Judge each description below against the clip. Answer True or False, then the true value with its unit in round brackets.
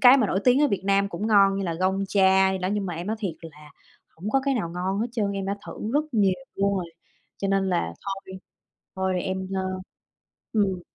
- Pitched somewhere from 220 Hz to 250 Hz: False (195 Hz)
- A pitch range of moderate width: False (1.6 semitones)